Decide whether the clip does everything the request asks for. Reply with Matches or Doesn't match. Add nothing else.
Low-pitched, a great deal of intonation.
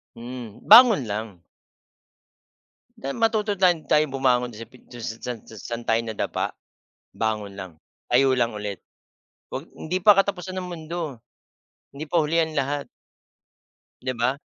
Matches